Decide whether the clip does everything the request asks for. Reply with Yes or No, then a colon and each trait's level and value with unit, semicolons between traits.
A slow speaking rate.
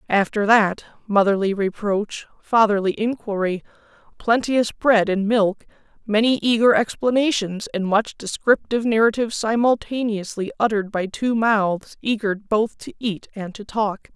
Yes: slow, 125 wpm